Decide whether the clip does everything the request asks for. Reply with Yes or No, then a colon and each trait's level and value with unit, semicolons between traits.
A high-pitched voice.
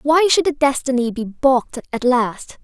Yes: very high, 265 Hz